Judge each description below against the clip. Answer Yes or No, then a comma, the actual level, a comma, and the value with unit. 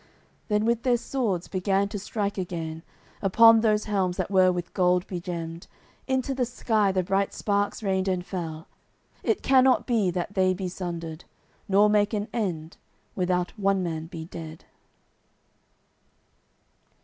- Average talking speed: Yes, average, 145 wpm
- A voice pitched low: No, high, 190 Hz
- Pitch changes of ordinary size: Yes, average, 3.0 semitones